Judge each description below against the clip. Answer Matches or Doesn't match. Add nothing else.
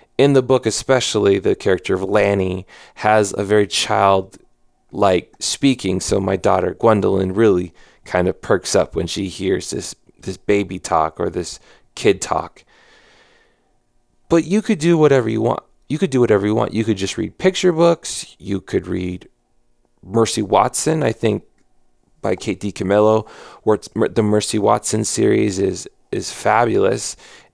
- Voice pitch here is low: Matches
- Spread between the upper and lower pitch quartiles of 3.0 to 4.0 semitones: Matches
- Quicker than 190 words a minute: Doesn't match